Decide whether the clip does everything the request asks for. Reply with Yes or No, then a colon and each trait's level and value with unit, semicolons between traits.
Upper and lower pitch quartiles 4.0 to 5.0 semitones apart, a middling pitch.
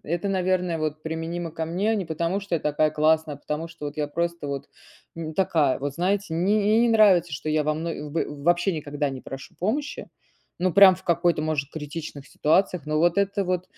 No: average, 3.3 semitones; medium, 165 Hz